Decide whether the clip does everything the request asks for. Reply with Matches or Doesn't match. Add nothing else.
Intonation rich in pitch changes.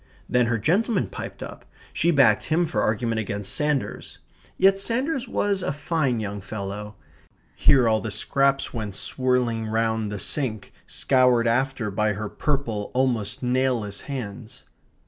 Doesn't match